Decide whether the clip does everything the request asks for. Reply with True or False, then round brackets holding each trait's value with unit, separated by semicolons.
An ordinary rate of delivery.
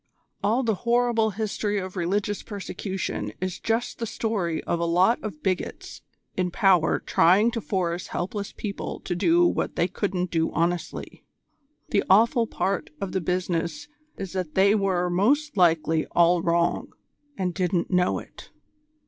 True (150 wpm)